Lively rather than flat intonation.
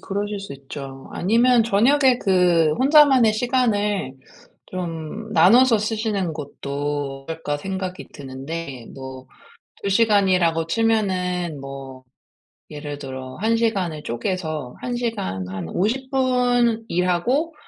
Yes: wide, 7.6 semitones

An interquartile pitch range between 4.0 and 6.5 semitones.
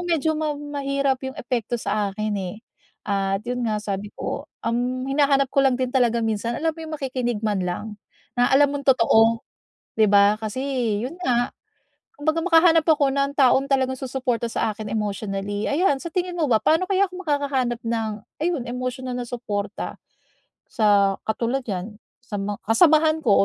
Yes: average, 4.8 semitones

